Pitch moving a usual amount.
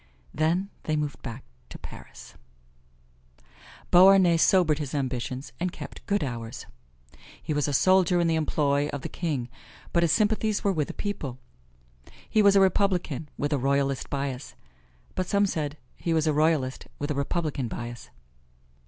Yes: average, 4.6 semitones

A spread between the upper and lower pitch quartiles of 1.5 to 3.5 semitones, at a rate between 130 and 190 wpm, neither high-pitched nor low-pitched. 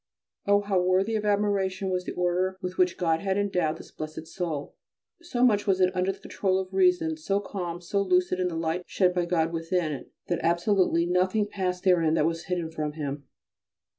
No: narrow, 2.6 semitones; average, 200 wpm; medium, 180 Hz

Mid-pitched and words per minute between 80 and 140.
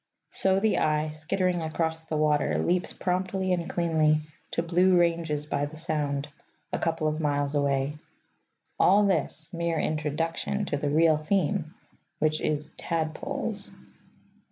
Yes: medium, 160 Hz; slow, 135 wpm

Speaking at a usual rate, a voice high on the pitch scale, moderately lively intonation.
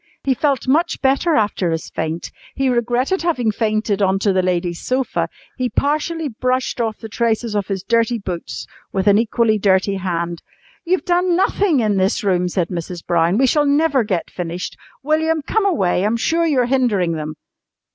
No: average, 175 wpm; high, 225 Hz; wide, 6.5 semitones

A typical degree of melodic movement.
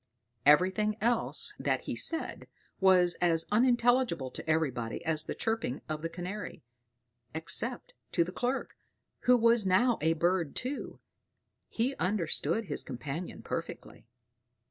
No: wide, 6.3 semitones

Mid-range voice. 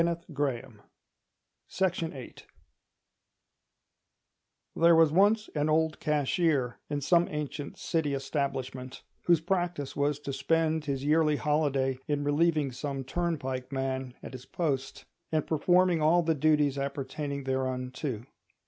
Yes: medium, 145 Hz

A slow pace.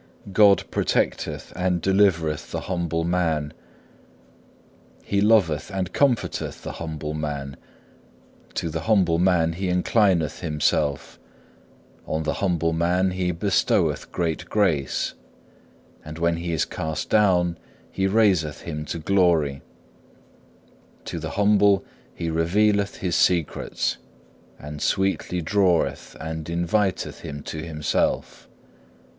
Yes: slow, 110 wpm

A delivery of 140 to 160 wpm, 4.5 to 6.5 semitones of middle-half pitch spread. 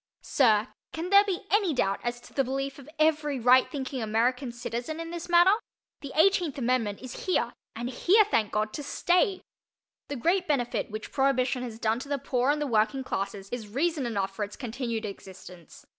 No: average, 190 wpm; average, 5.3 semitones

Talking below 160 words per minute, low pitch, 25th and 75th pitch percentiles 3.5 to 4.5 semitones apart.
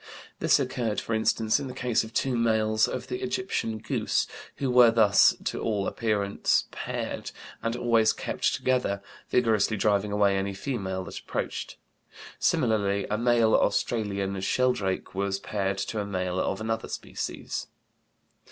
No: average, 145 wpm; low, 110 Hz; average, 2.7 semitones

